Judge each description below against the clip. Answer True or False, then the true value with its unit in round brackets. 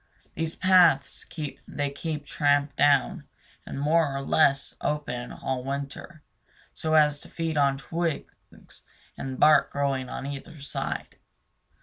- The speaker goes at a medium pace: False (130 wpm)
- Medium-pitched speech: True (145 Hz)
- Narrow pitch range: True (2.3 semitones)